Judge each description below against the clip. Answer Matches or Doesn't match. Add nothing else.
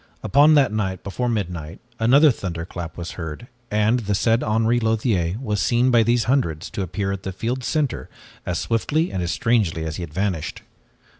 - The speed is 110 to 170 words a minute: Doesn't match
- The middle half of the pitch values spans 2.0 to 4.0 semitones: Doesn't match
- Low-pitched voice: Matches